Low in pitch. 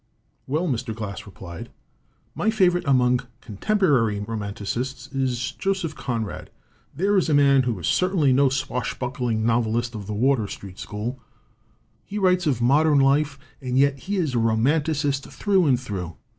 Yes: low, 130 Hz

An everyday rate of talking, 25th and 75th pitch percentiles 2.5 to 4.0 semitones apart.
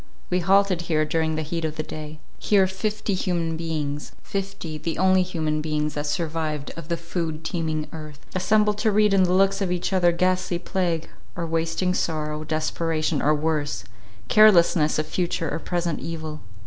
Yes: average, 170 wpm; average, 3.0 semitones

